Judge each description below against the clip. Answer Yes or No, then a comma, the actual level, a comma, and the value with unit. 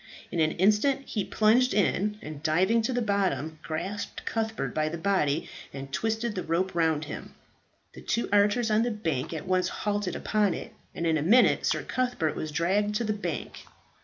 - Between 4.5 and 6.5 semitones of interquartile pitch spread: Yes, average, 5.1 semitones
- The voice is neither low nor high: No, high, 200 Hz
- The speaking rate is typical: Yes, average, 190 wpm